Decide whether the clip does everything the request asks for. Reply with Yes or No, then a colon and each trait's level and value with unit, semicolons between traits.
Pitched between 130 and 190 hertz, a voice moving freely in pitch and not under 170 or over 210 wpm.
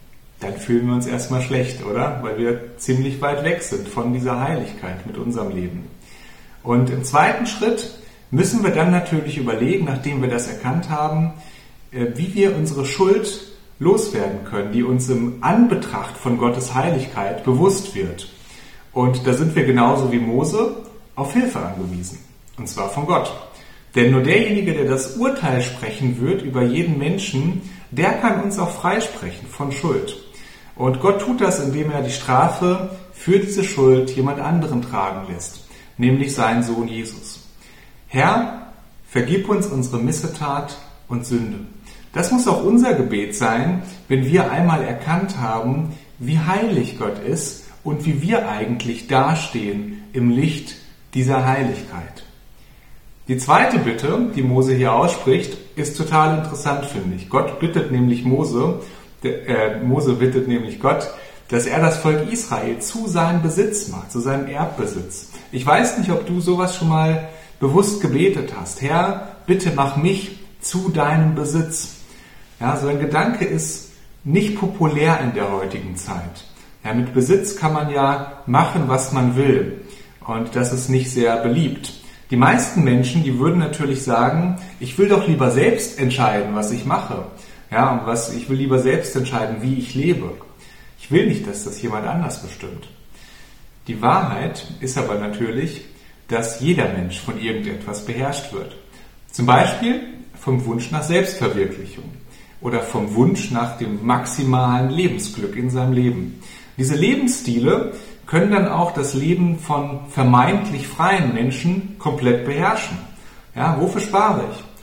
No: low, 135 Hz; wide, 6.0 semitones; average, 150 wpm